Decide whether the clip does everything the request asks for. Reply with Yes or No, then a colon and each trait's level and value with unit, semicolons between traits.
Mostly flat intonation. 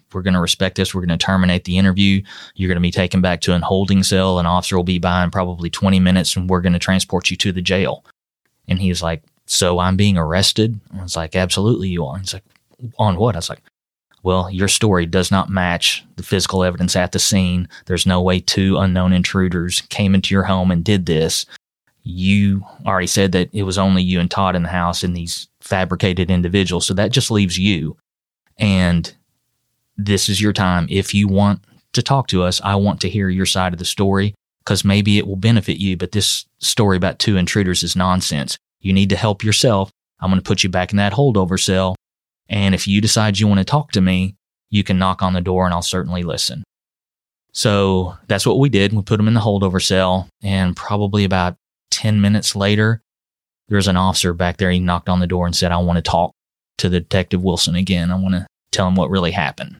Yes: narrow, 1.7 semitones